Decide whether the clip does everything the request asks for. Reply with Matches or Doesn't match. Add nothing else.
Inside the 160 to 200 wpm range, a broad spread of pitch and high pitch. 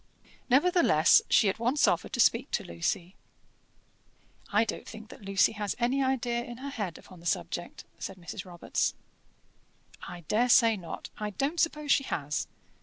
Matches